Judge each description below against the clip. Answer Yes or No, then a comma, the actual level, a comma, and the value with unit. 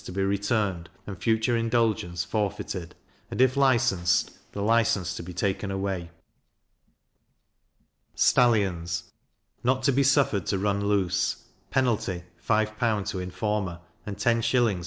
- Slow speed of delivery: Yes, slow, 120 wpm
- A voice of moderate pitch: No, low, 105 Hz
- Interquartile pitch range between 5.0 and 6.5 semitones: No, average, 3.9 semitones